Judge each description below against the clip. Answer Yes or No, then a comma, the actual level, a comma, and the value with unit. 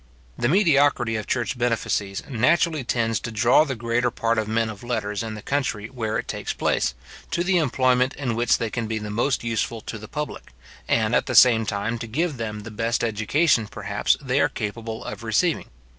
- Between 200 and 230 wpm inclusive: Yes, fast, 205 wpm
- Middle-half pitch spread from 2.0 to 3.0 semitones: Yes, average, 2.7 semitones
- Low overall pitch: Yes, low, 115 Hz